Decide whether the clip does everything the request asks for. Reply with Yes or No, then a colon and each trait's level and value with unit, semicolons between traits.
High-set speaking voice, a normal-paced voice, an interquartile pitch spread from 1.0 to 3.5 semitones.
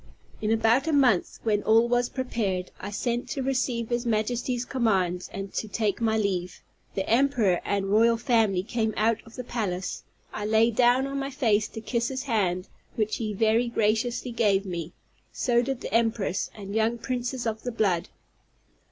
Yes: high, 225 Hz; average, 180 wpm; average, 2.9 semitones